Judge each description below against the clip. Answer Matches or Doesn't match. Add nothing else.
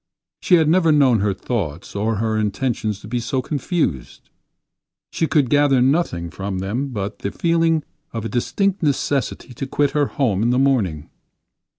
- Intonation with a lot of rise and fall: Matches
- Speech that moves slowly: Doesn't match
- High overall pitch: Doesn't match